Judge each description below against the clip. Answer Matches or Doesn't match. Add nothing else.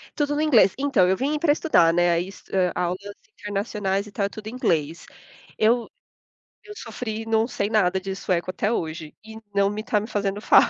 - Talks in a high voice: Matches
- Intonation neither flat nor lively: Matches